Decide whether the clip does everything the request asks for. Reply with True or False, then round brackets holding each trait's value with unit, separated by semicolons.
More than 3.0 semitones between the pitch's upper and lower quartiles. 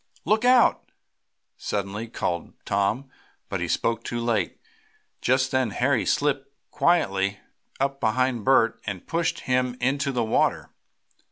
True (3.9 semitones)